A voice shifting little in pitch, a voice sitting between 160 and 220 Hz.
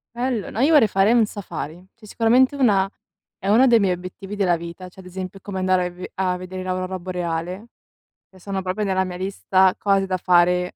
Yes: narrow, 2.1 semitones; high, 190 Hz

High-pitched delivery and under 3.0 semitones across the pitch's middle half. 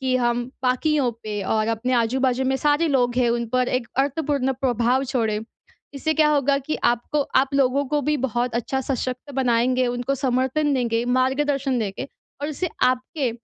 Yes: very high, 255 Hz; narrow, 2.4 semitones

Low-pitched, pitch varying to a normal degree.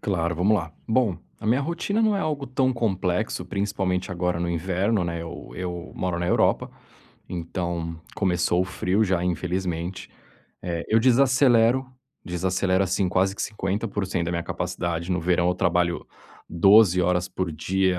Yes: very low, 90 Hz; average, 3.4 semitones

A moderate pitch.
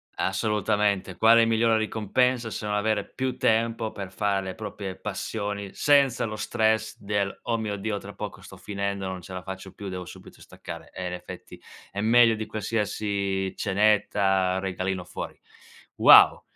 No: low, 105 Hz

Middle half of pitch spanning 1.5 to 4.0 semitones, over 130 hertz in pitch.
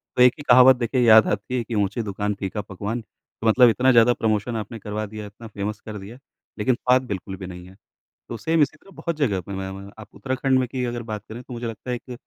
No: average, 3.3 semitones; low, 115 Hz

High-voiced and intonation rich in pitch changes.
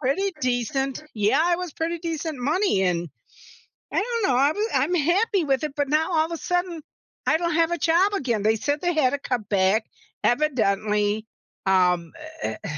Yes: very high, 285 Hz; wide, 7.4 semitones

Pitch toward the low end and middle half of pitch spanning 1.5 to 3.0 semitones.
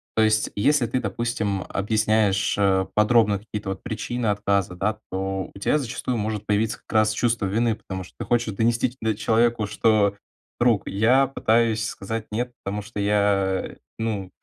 Yes: low, 110 Hz; narrow, 2.4 semitones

